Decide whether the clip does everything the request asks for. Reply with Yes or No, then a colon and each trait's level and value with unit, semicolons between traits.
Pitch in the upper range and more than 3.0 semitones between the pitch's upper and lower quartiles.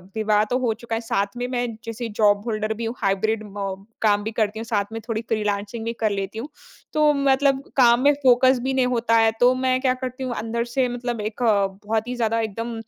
No: high, 230 Hz; narrow, 2.5 semitones